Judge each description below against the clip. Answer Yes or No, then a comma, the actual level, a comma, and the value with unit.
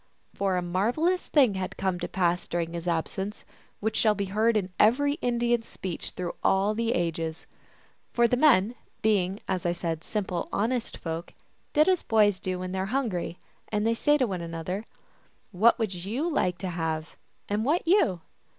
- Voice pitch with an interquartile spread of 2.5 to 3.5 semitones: No, average, 4.6 semitones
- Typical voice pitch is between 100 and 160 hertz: No, high, 195 Hz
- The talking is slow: No, average, 185 wpm